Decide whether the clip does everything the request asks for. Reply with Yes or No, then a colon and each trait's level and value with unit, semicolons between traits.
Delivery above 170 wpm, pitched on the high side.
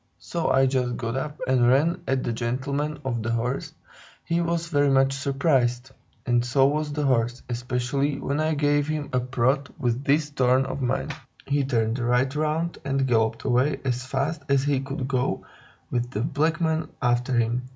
No: average, 180 wpm; low, 135 Hz